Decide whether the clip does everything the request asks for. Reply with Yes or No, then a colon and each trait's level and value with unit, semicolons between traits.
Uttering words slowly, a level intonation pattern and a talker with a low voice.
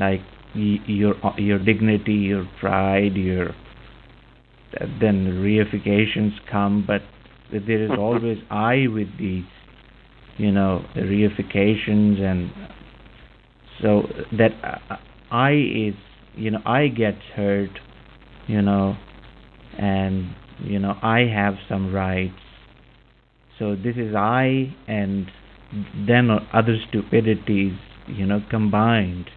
Yes: slow, 110 wpm; narrow, 2.1 semitones; low, 105 Hz